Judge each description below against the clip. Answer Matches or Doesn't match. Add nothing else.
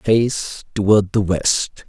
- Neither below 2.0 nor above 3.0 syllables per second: Matches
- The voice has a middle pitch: Doesn't match